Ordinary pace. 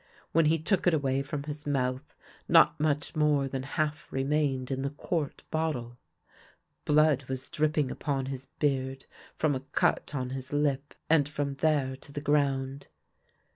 Yes: average, 160 wpm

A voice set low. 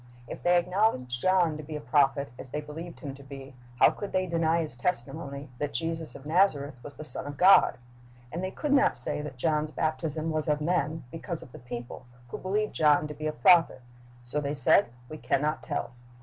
No: medium, 150 Hz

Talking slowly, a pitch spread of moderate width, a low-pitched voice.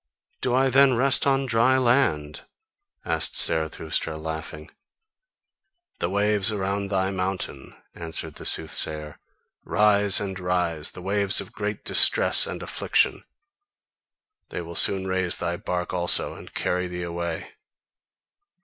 Yes: slow, 125 wpm; average, 3.7 semitones; very low, 95 Hz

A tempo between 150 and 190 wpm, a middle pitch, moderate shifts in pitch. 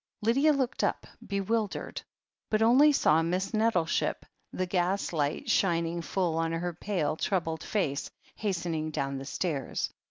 No: average, 140 wpm; medium, 175 Hz; average, 4.5 semitones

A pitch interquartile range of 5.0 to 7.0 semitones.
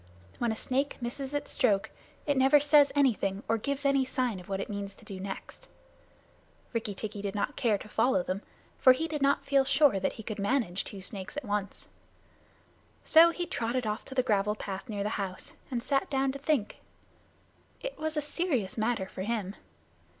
Yes: wide, 5.5 semitones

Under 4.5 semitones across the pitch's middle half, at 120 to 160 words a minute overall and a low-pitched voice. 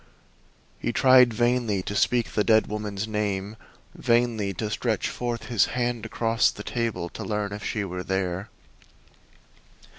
Yes: average, 2.9 semitones; average, 145 wpm; low, 110 Hz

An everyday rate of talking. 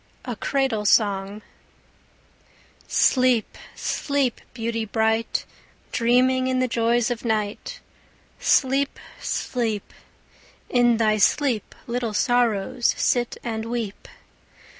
No: slow, 95 wpm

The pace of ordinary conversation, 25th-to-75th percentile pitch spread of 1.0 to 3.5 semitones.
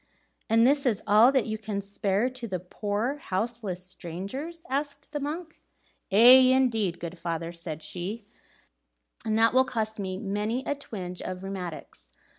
No: average, 155 wpm; wide, 5.6 semitones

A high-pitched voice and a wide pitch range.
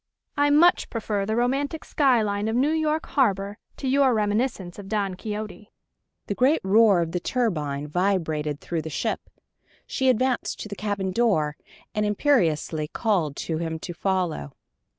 Yes: high, 205 Hz; wide, 6.1 semitones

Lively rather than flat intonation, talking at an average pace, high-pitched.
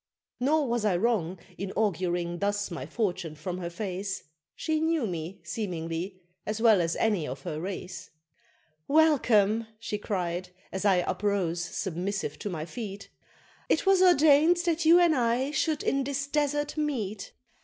Yes: wide, 7.6 semitones; average, 155 wpm; high, 205 Hz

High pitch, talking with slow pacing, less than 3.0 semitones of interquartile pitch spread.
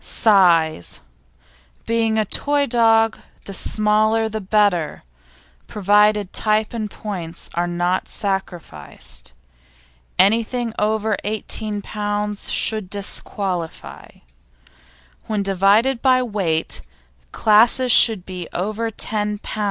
Yes: high, 210 Hz; slow, 95 wpm; narrow, 2.5 semitones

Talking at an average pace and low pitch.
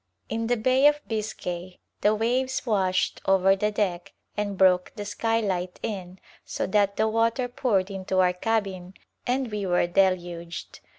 No: average, 155 wpm; high, 200 Hz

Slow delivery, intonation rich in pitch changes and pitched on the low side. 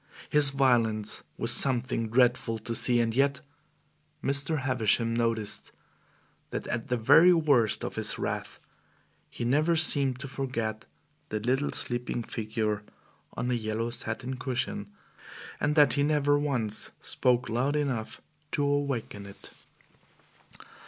No: slow, 130 wpm; average, 3.6 semitones; low, 125 Hz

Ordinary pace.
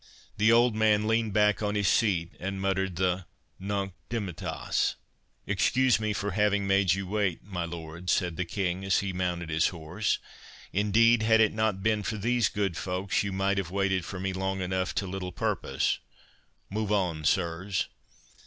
Yes: average, 170 wpm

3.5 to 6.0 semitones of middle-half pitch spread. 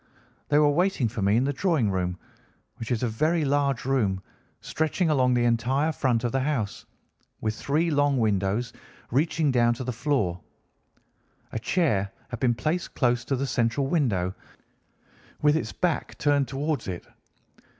Yes: average, 4.4 semitones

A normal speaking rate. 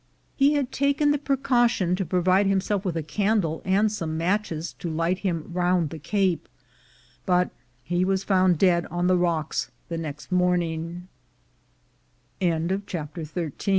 No: slow, 130 wpm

